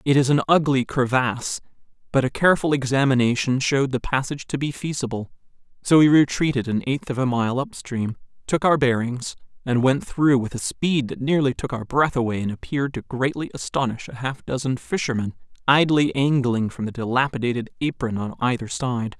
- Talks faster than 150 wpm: Yes, average, 180 wpm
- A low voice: Yes, low, 130 Hz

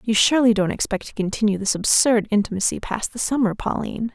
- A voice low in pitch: No, high, 215 Hz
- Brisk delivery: No, average, 190 wpm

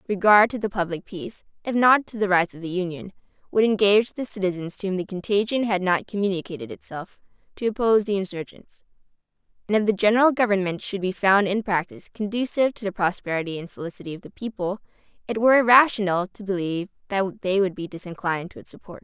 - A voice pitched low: No, high, 195 Hz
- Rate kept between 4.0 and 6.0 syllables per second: No, 6.5 syllables/s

